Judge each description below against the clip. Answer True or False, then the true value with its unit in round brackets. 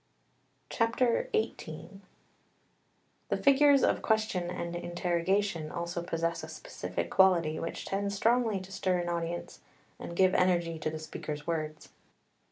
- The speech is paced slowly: True (125 wpm)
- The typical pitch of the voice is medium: True (180 Hz)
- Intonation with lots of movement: False (3.3 semitones)